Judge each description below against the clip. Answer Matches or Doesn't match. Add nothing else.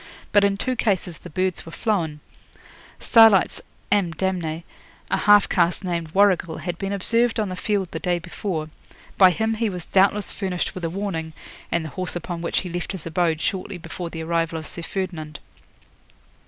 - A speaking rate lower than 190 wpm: Matches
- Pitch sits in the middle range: Matches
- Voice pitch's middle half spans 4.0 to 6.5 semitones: Doesn't match